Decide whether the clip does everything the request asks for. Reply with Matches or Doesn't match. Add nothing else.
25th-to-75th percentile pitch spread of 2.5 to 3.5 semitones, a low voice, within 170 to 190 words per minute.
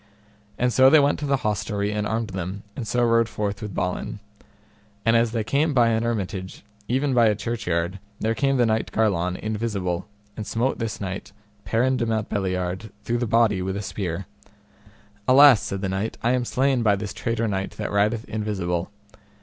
Matches